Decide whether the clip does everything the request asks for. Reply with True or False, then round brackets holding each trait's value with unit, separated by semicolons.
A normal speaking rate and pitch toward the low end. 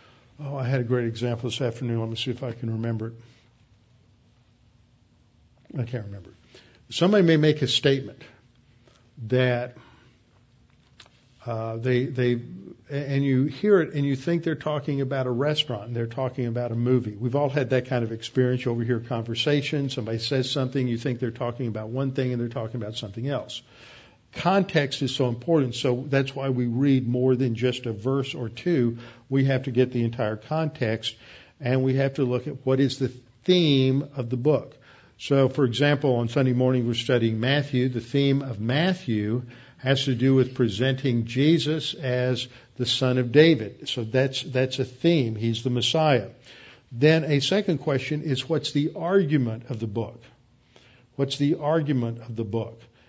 True (180 wpm; 125 Hz)